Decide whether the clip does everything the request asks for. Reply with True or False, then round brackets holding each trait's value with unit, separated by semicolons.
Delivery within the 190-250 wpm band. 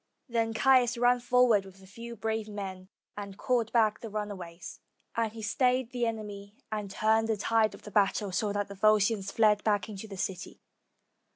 True (195 wpm)